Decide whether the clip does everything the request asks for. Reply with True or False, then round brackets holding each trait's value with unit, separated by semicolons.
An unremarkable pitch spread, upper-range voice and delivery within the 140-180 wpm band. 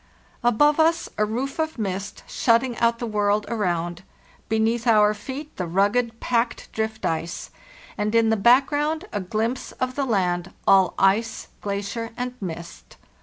True (3.7 semitones; 220 Hz; 150 wpm)